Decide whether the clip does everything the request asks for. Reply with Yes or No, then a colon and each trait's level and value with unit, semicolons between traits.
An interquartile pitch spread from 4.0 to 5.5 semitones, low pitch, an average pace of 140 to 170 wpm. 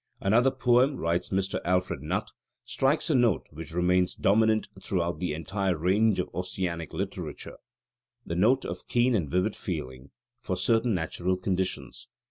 Yes: average, 4.4 semitones; very low, 95 Hz; average, 145 wpm